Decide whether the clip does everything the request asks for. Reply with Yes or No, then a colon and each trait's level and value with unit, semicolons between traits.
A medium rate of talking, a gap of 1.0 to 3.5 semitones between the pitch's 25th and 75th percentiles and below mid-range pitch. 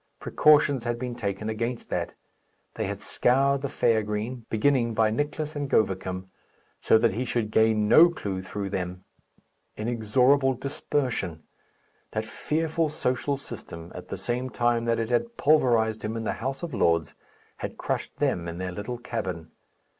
No: average, 160 wpm; average, 4.1 semitones; low, 115 Hz